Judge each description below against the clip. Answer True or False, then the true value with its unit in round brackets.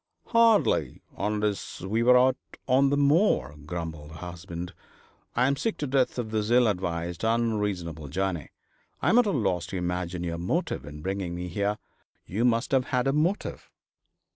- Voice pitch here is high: False (105 Hz)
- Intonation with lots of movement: True (6.4 semitones)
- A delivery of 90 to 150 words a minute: False (170 wpm)